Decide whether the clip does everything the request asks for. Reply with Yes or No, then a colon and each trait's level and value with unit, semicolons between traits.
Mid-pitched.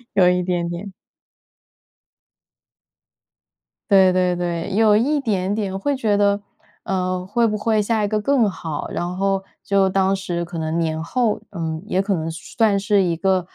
No: high, 195 Hz